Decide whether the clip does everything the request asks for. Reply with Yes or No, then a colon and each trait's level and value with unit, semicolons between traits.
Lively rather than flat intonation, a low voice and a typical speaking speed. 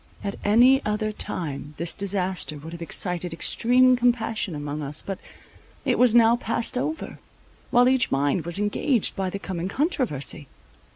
No: wide, 6.3 semitones; high, 200 Hz; average, 155 wpm